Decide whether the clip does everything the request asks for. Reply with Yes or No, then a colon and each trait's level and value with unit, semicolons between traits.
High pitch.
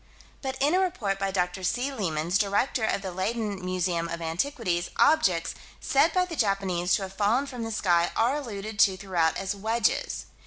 Yes: high, 200 Hz